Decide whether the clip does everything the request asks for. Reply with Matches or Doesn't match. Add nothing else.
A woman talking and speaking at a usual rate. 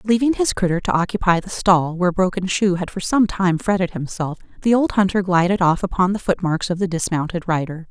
Doesn't match